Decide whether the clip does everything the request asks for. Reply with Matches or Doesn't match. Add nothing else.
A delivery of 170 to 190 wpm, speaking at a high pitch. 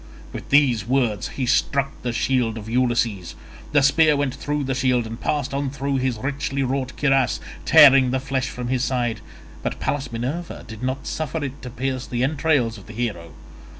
Doesn't match